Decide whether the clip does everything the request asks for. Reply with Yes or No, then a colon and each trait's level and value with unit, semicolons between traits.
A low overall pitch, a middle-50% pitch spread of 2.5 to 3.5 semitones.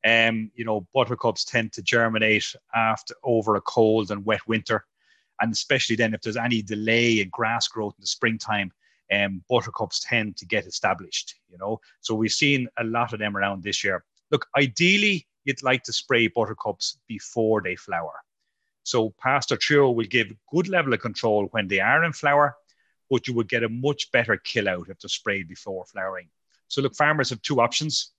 Yes: low, 115 Hz; average, 2.9 semitones